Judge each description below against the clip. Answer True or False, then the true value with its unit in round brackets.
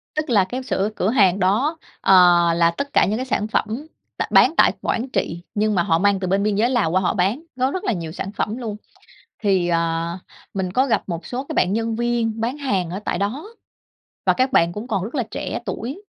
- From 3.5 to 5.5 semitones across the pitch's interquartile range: True (5.2 semitones)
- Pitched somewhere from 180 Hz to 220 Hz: True (210 Hz)